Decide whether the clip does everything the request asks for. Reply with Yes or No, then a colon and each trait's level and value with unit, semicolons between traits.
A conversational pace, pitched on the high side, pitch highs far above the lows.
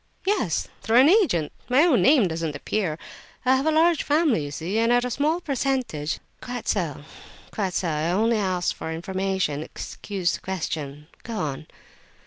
Yes: average, 165 wpm; high, 200 Hz; wide, 8.3 semitones